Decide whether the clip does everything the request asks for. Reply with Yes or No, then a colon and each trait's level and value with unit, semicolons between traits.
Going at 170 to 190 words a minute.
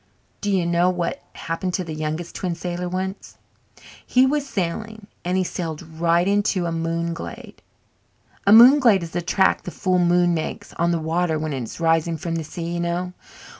Yes: average, 185 wpm